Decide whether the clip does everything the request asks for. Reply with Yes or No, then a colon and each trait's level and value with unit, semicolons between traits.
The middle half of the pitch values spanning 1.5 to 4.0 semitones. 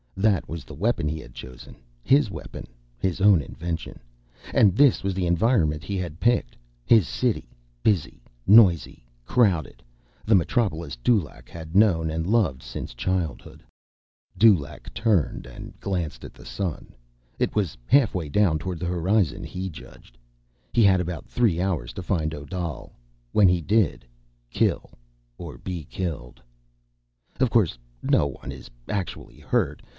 No: average, 4.6 semitones